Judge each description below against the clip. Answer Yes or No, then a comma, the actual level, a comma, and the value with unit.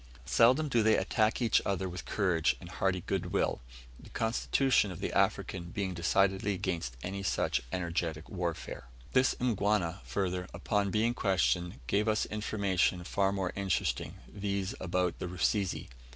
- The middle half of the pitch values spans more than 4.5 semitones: No, average, 3.0 semitones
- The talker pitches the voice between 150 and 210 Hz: No, very low, 95 Hz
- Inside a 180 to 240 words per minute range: No, average, 145 wpm